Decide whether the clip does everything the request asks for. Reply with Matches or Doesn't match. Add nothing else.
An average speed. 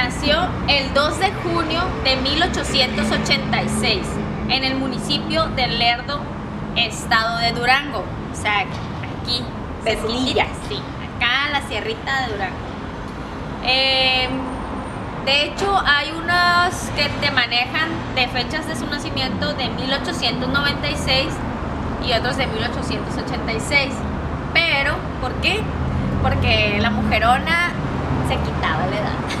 Doesn't match